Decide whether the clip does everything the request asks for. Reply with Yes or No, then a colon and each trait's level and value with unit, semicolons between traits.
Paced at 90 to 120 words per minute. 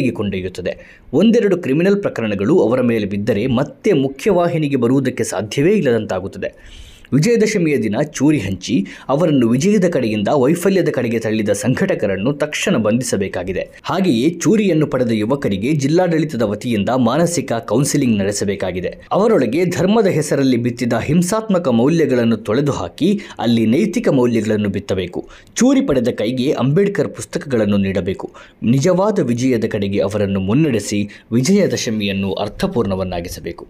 Yes: fast, 105 wpm